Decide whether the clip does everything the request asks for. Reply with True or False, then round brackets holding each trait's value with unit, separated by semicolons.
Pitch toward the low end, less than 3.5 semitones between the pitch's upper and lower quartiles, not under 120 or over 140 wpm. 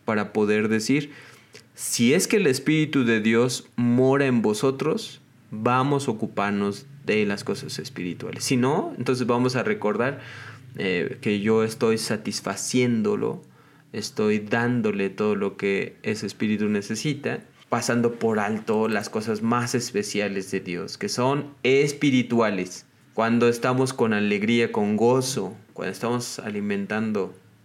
True (115 Hz; 3.1 semitones; 130 wpm)